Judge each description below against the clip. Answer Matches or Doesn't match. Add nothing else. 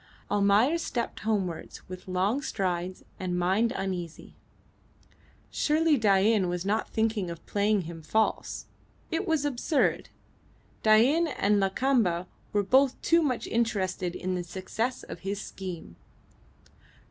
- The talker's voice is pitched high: Matches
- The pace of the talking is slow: Matches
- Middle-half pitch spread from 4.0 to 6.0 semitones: Matches